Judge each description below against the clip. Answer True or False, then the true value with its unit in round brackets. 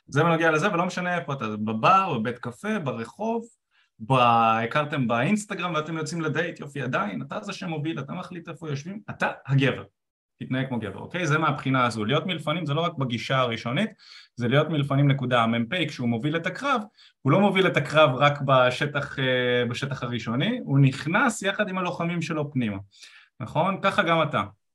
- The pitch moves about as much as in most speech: False (5.8 semitones)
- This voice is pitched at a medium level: True (150 Hz)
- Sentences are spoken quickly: True (170 wpm)